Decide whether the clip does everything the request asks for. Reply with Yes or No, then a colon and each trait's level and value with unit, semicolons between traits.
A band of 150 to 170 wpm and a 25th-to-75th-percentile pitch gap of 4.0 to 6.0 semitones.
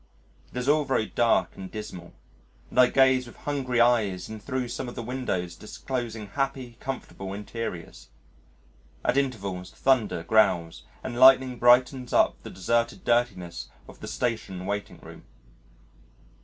No: average, 140 wpm; average, 4.4 semitones